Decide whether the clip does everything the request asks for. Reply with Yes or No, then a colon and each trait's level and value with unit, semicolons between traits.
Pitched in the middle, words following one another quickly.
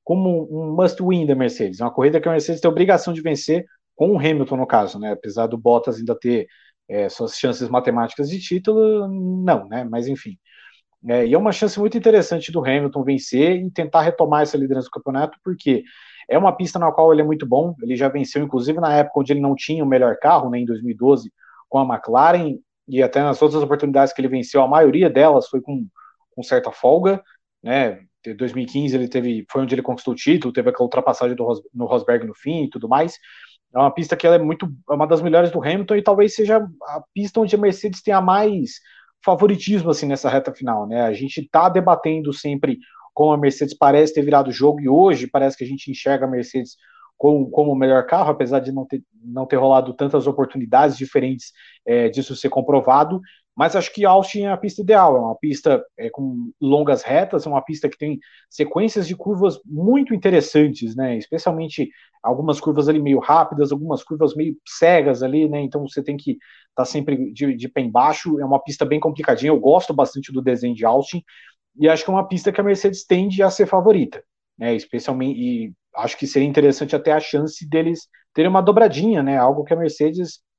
Yes: medium, 150 Hz; fast, 210 wpm